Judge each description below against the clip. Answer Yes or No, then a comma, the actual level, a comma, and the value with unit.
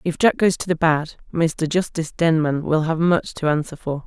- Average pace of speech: No, fast, 220 wpm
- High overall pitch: No, medium, 160 Hz